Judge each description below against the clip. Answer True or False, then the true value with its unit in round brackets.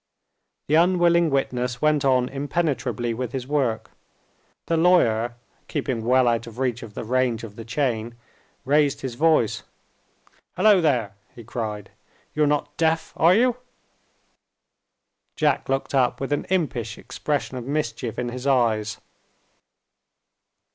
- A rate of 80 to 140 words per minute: True (135 wpm)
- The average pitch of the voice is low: True (130 Hz)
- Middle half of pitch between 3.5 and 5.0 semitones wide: True (4.3 semitones)